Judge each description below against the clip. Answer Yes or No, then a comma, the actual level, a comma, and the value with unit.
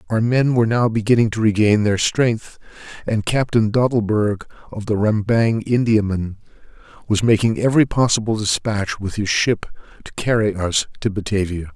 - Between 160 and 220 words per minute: No, average, 150 wpm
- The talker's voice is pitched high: No, low, 110 Hz